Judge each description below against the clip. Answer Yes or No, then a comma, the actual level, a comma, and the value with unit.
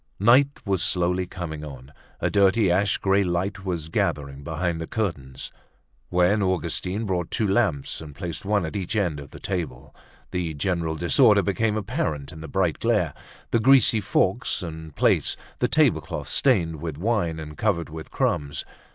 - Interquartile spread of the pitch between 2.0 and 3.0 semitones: No, average, 4.2 semitones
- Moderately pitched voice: No, very low, 90 Hz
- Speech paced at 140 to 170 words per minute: Yes, average, 165 wpm